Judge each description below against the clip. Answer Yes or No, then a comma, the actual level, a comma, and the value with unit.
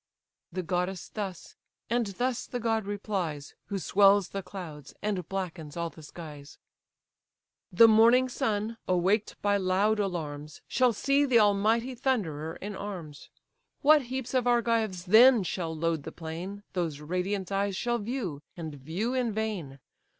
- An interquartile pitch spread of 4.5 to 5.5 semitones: Yes, average, 5.1 semitones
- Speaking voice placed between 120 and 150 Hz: No, high, 195 Hz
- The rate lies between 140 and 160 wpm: Yes, average, 145 wpm